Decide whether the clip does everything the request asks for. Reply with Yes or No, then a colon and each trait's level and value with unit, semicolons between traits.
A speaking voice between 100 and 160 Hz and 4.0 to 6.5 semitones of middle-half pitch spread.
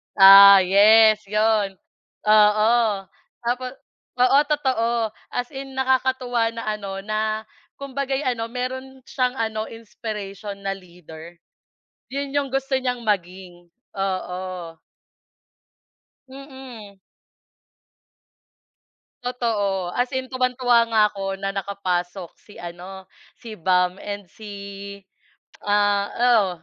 No: high, 215 Hz; average, 4.4 semitones